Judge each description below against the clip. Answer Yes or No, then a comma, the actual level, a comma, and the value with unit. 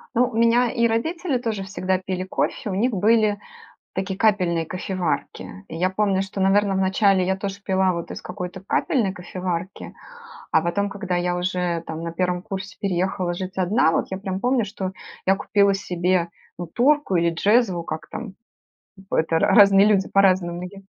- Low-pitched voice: No, high, 190 Hz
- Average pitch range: No, narrow, 2.3 semitones